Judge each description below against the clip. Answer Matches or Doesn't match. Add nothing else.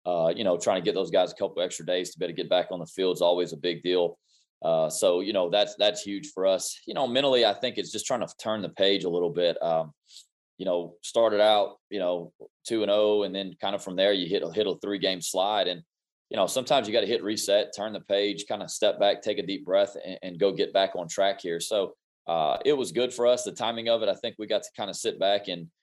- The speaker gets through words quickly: Matches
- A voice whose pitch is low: Matches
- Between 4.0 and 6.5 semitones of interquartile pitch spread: Matches